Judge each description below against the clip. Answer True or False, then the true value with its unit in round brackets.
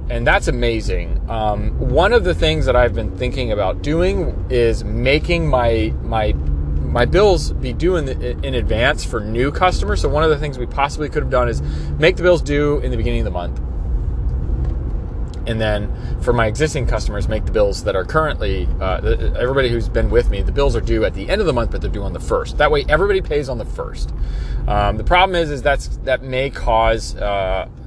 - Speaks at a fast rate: True (215 wpm)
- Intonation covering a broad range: True (6.0 semitones)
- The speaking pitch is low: True (110 Hz)